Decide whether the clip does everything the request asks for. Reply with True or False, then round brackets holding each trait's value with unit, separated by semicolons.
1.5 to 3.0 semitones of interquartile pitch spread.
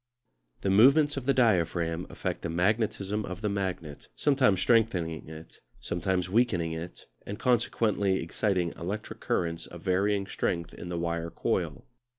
False (4.1 semitones)